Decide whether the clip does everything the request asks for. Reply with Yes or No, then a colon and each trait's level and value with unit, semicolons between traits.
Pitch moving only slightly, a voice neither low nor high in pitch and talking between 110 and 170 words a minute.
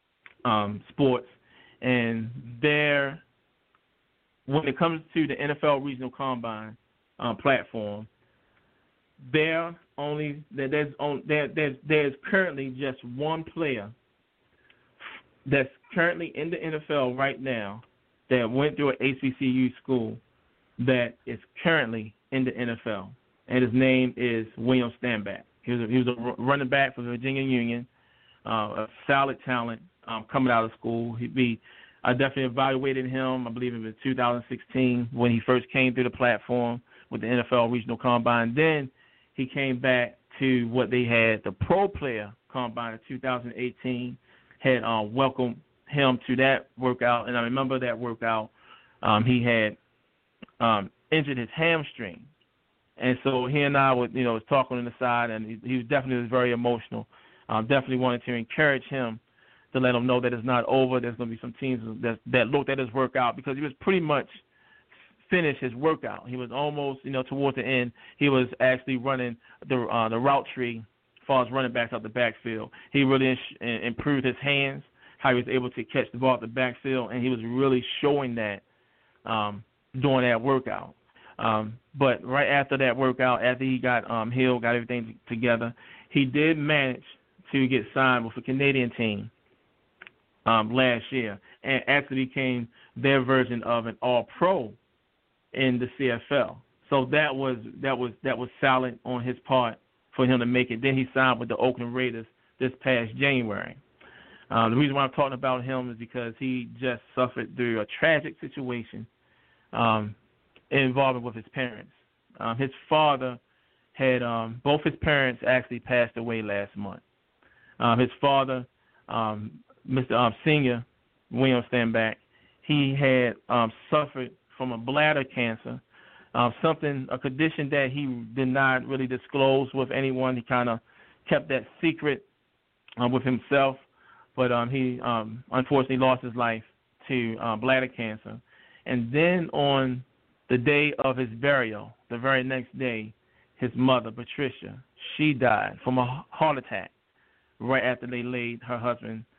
No: narrow, 2.2 semitones; low, 125 Hz; average, 165 wpm